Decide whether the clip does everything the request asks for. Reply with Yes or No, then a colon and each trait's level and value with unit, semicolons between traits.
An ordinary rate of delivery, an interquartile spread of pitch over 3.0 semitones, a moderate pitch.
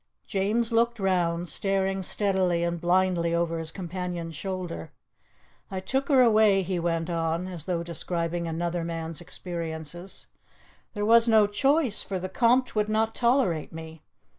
Yes: average, 145 wpm; average, 3.7 semitones; medium, 180 Hz